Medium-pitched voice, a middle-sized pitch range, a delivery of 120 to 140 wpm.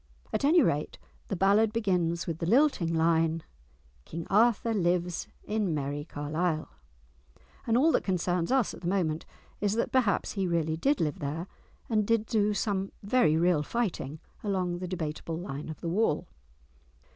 No: medium, 180 Hz; average, 4.7 semitones; average, 160 wpm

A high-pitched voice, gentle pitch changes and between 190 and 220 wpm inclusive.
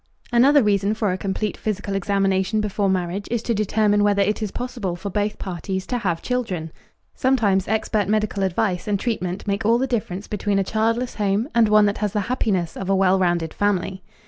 Yes: high, 205 Hz; narrow, 2.3 semitones; average, 200 wpm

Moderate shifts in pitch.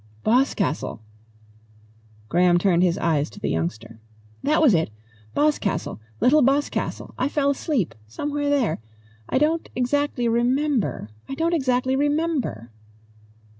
No: wide, 8.8 semitones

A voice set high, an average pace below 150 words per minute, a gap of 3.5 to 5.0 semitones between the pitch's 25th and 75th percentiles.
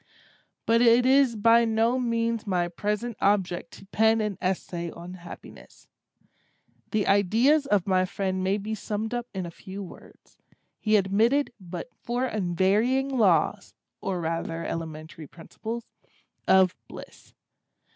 Yes: high, 205 Hz; slow, 135 wpm; average, 4.0 semitones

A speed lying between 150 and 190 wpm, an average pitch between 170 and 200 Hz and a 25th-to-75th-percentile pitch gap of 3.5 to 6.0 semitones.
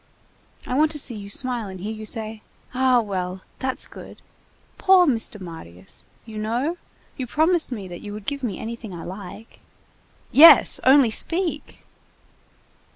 No: average, 155 wpm; high, 225 Hz; average, 4.9 semitones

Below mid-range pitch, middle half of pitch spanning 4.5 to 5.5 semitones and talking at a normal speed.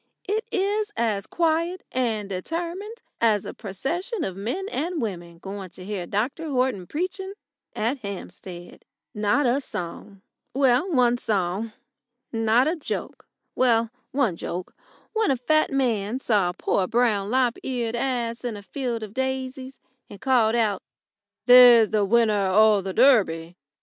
No: high, 235 Hz; average, 5.0 semitones; average, 145 wpm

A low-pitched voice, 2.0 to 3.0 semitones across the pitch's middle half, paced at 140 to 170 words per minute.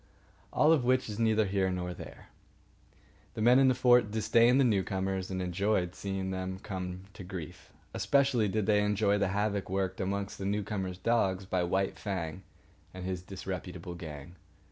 Yes: very low, 95 Hz; narrow, 2.6 semitones; average, 165 wpm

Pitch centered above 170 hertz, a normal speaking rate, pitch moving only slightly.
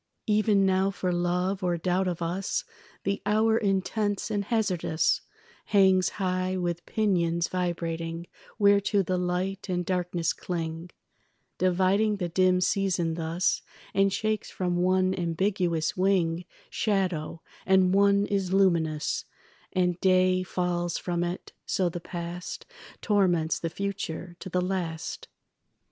No: medium, 185 Hz; slow, 125 wpm; narrow, 2.0 semitones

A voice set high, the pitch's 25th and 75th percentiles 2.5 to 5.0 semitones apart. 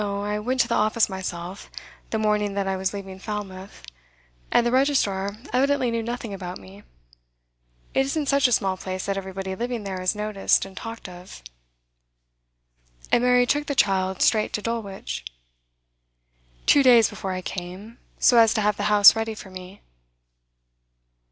Yes: high, 210 Hz; average, 3.5 semitones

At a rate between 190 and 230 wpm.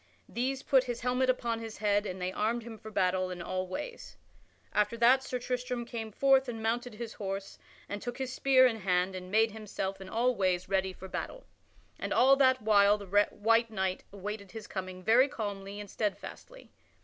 Yes: average, 195 wpm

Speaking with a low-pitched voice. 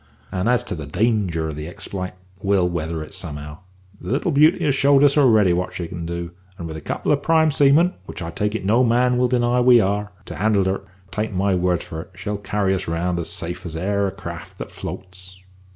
Yes: very low, 95 Hz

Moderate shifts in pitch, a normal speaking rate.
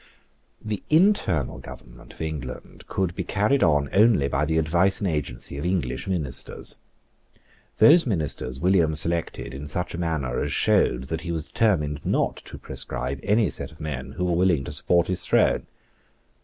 Yes: average, 4.8 semitones; average, 170 wpm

